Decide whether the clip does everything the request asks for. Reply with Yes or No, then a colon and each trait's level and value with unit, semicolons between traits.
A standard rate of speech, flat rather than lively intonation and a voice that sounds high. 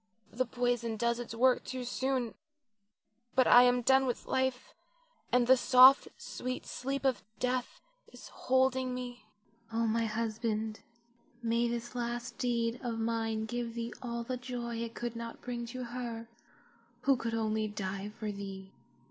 Yes: average, 155 wpm; narrow, 1.7 semitones; high, 235 Hz